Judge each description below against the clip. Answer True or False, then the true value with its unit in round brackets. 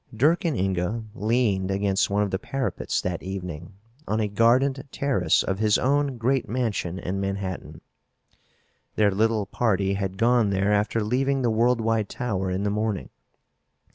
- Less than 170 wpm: True (155 wpm)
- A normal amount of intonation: True (3.8 semitones)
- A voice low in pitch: True (105 Hz)